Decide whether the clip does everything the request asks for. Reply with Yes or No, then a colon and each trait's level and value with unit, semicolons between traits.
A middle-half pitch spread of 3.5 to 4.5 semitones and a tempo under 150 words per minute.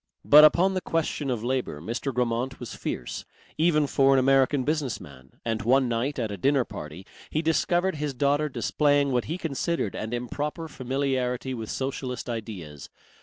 No: average, 4.0 semitones; average, 170 wpm